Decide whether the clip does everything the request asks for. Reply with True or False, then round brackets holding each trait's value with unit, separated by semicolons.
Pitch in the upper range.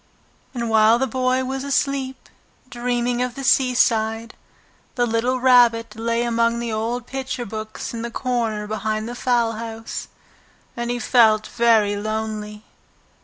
True (235 Hz)